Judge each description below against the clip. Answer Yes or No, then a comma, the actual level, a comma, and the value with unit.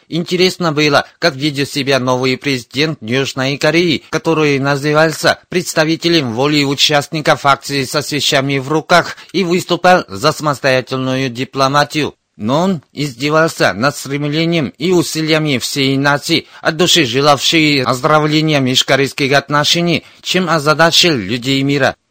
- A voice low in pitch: No, medium, 145 Hz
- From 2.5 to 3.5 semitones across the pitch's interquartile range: Yes, average, 2.9 semitones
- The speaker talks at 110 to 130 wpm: Yes, average, 115 wpm